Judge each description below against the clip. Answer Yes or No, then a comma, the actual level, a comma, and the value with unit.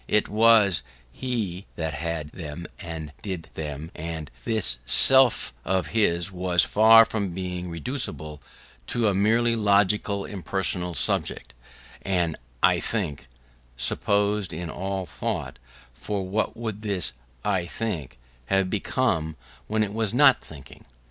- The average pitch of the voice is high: No, very low, 95 Hz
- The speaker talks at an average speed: No, slow, 130 wpm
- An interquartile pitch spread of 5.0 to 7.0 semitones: No, average, 4.6 semitones